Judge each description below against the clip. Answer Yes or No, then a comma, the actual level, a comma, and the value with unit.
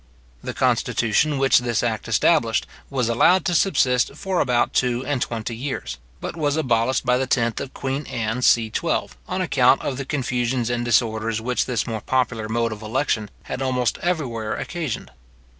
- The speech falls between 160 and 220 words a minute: Yes, average, 170 wpm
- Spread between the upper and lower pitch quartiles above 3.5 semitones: No, average, 2.8 semitones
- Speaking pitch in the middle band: No, low, 125 Hz